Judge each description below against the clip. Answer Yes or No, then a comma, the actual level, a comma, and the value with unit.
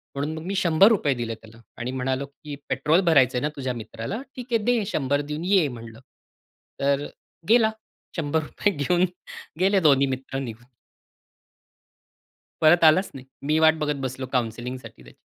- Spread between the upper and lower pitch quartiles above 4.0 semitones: Yes, average, 4.8 semitones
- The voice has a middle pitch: Yes, medium, 145 Hz